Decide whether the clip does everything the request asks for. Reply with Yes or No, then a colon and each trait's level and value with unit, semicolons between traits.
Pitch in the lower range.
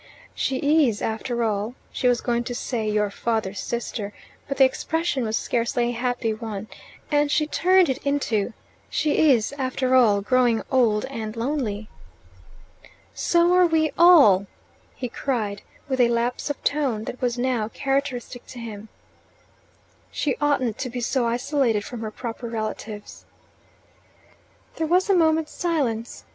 No: high, 245 Hz